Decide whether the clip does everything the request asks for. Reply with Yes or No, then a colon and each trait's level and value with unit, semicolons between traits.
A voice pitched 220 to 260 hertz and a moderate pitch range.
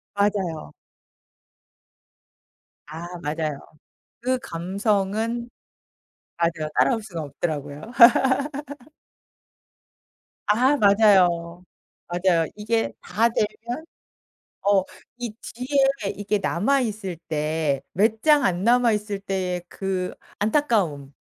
No: high, 200 Hz; average, 5.0 semitones